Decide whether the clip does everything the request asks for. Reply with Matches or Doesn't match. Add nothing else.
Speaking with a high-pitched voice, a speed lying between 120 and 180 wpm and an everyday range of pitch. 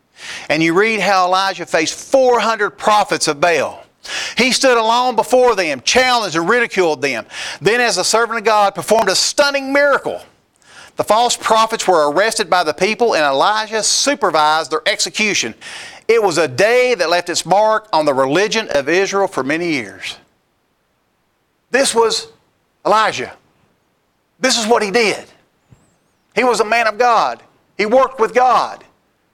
Matches